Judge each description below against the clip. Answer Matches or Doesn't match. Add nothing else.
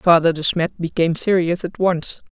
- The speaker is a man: Doesn't match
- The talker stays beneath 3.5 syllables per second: Doesn't match